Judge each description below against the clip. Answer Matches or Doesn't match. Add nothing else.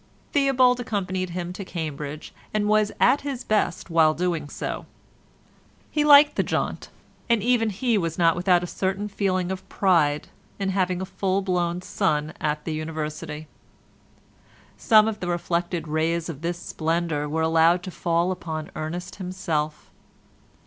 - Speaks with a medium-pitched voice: Matches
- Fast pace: Doesn't match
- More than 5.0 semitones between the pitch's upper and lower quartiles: Doesn't match